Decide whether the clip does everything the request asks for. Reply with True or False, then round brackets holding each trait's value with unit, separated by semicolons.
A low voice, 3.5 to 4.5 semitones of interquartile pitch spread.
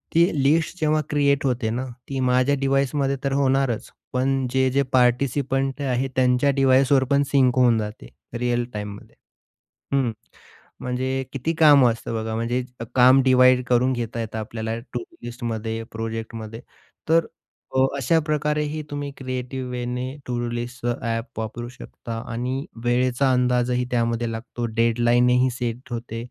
False (125 Hz; 2.4 semitones)